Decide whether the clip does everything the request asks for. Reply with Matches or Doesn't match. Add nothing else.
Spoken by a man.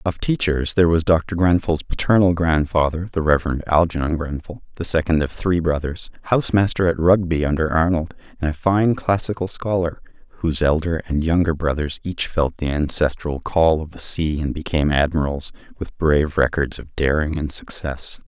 Matches